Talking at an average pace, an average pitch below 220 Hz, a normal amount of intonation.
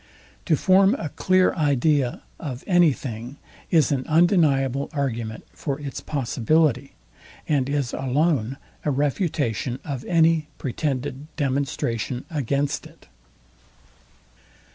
No: slow, 105 wpm; medium, 140 Hz; average, 3.3 semitones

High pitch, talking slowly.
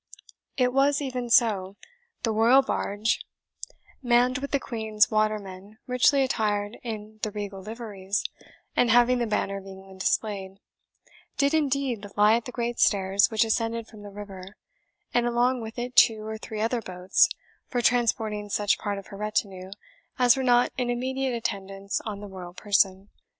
No: high, 220 Hz; average, 160 wpm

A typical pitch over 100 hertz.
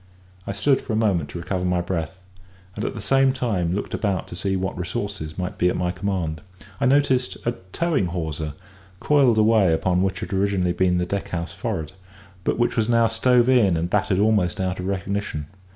No: very low, 95 Hz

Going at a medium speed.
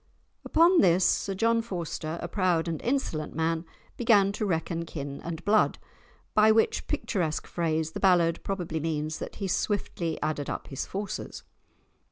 Yes: average, 155 wpm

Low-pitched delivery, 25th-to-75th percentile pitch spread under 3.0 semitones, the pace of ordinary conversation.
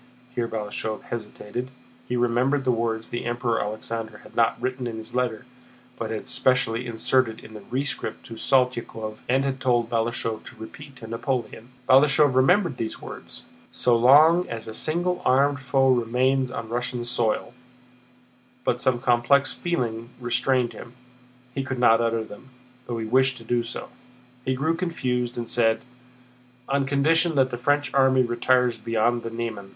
Yes: low, 120 Hz; narrow, 2.4 semitones; average, 160 wpm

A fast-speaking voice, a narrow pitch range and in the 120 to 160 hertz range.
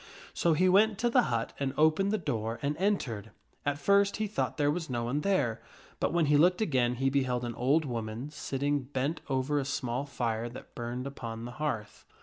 No: fast, 210 wpm; average, 5.0 semitones; medium, 140 Hz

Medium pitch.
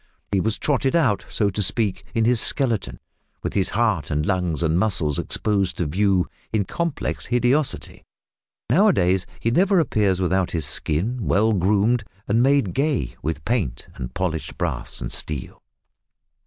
No: low, 100 Hz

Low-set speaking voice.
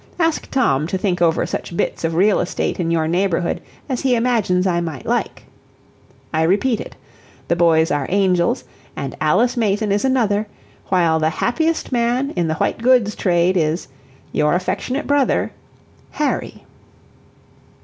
No: medium, 185 Hz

